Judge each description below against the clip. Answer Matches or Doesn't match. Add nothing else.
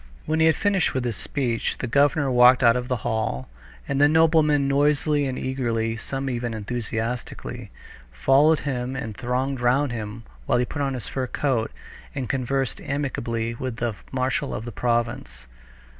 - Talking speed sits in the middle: Matches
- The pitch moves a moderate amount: Matches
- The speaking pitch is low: Matches